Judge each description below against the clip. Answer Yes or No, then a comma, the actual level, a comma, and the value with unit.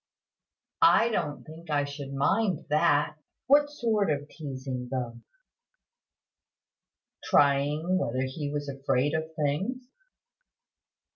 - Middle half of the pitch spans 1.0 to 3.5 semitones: No, average, 4.2 semitones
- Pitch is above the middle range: No, medium, 145 Hz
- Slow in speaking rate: Yes, slow, 100 wpm